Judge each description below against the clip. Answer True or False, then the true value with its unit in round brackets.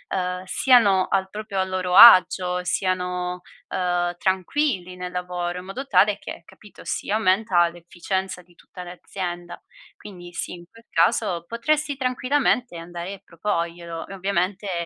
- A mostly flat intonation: True (2.3 semitones)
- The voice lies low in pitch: False (185 Hz)